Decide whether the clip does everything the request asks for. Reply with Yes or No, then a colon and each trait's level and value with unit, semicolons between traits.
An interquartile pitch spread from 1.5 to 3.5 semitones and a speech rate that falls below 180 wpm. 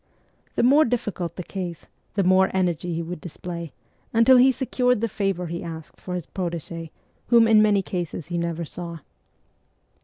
No: average, 4.0 semitones; average, 165 wpm